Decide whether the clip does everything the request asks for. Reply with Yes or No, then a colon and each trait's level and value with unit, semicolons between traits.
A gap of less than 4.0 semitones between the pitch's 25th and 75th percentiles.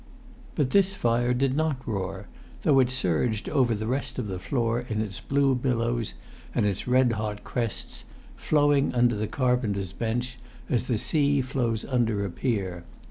Yes: average, 3.5 semitones